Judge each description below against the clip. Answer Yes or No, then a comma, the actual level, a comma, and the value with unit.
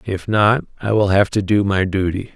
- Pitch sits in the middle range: No, low, 100 Hz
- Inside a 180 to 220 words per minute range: Yes, fast, 205 wpm